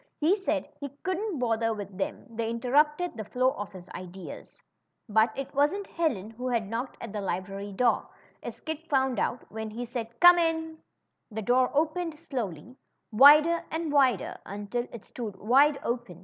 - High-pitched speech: Yes, high, 245 Hz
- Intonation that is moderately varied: No, wide, 5.9 semitones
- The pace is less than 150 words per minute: No, average, 175 wpm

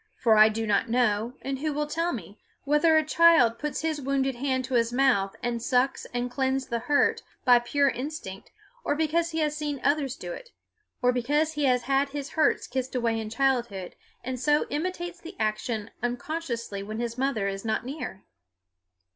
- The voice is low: No, very high, 260 Hz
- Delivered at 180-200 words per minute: Yes, average, 190 wpm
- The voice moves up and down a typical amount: Yes, average, 4.2 semitones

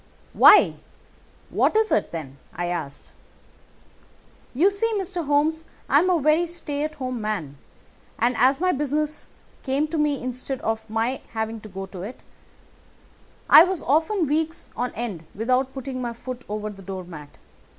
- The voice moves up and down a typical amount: No, wide, 6.2 semitones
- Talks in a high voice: Yes, very high, 255 Hz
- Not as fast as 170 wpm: Yes, average, 160 wpm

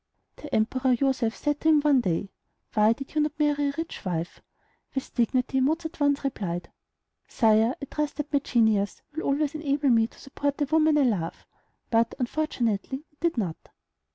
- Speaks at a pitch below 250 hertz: No, very high, 275 Hz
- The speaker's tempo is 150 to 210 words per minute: Yes, average, 180 wpm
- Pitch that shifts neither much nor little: Yes, average, 4.7 semitones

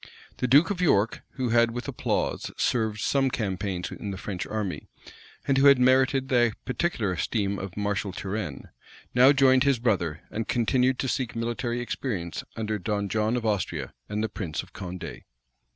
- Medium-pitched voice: No, low, 115 Hz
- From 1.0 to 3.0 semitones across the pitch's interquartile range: No, average, 4.2 semitones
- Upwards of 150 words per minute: Yes, average, 170 wpm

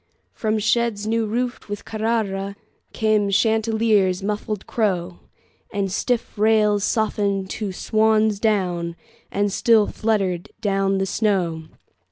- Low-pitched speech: No, high, 210 Hz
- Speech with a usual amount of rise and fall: No, narrow, 2.1 semitones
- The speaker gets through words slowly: Yes, slow, 100 wpm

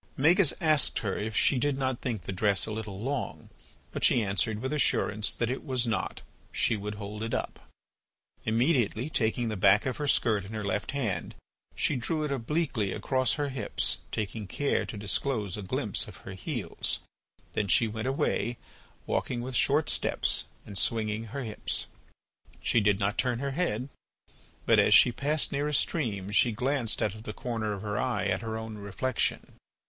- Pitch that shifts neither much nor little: Yes, average, 4.2 semitones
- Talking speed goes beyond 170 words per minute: Yes, average, 185 wpm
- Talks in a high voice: No, low, 115 Hz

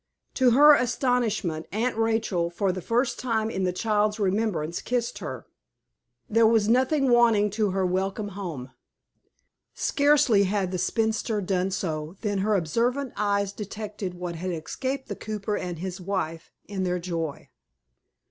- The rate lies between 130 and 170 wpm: Yes, average, 145 wpm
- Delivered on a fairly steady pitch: No, average, 3.8 semitones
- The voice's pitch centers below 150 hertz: No, high, 205 Hz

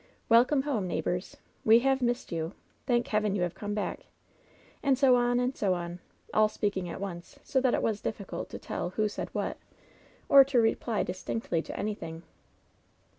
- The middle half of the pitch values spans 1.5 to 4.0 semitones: No, average, 5.1 semitones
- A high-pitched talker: Yes, high, 215 Hz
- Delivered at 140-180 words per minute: No, average, 190 wpm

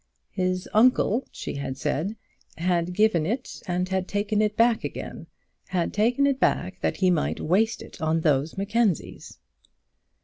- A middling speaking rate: Yes, average, 150 wpm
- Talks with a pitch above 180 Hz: Yes, high, 190 Hz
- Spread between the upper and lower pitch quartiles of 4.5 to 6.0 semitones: No, average, 4.1 semitones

